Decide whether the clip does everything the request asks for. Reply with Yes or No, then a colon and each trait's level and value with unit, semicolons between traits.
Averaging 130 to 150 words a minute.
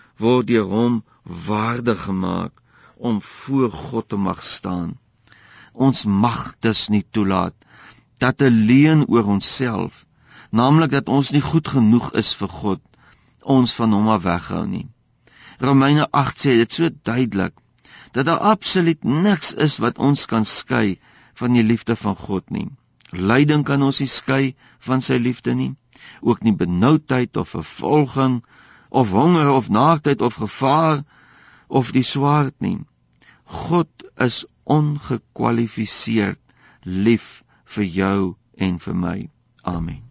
Yes: average, 135 wpm